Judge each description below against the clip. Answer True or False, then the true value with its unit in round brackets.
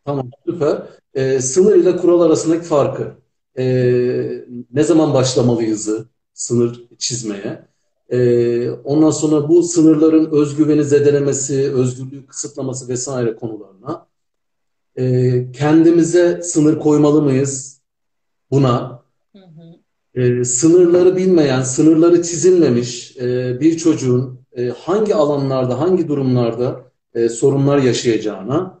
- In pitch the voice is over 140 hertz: False (135 Hz)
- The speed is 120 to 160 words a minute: False (100 wpm)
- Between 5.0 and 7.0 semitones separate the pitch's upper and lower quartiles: False (4.2 semitones)